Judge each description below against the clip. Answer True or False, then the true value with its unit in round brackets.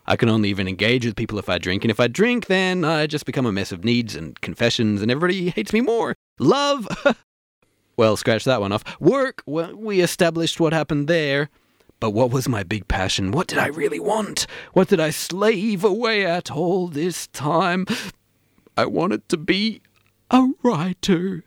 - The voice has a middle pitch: True (160 Hz)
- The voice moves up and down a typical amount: False (8.7 semitones)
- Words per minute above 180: True (190 wpm)